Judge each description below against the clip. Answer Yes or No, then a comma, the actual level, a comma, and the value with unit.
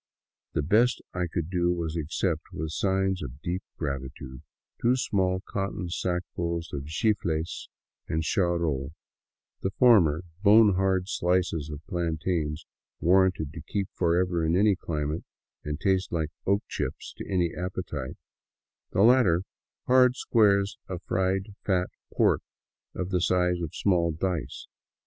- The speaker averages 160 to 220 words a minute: No, average, 140 wpm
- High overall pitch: No, very low, 90 Hz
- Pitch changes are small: No, average, 3.2 semitones